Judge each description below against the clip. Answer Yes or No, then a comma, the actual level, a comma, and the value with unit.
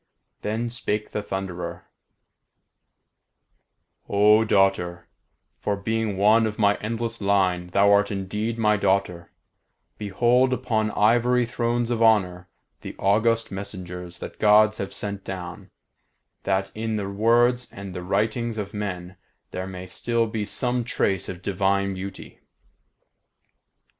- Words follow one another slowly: Yes, slow, 125 wpm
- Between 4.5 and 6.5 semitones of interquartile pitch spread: No, average, 2.8 semitones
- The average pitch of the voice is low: Yes, low, 105 Hz